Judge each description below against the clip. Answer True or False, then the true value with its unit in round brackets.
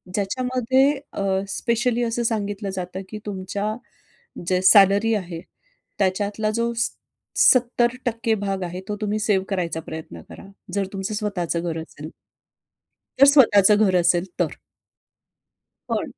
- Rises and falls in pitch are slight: False (3.6 semitones)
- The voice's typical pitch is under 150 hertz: False (205 Hz)